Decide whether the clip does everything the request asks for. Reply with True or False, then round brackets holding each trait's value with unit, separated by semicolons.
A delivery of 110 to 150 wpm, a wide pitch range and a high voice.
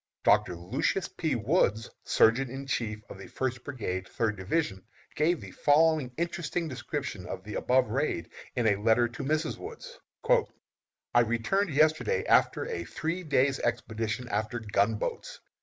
False (145 wpm; 6.2 semitones; 125 Hz)